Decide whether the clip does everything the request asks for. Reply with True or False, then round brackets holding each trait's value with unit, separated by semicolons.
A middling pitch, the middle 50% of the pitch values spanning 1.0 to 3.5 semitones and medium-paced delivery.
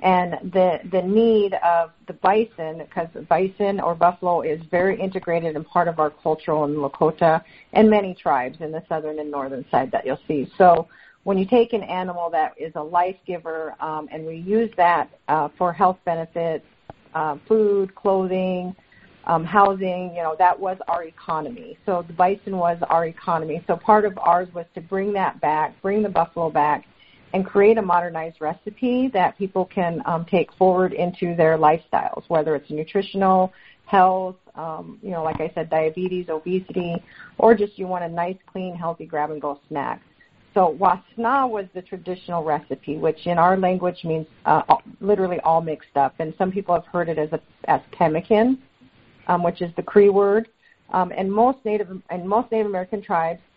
True (175 Hz; 3.2 semitones; 180 wpm)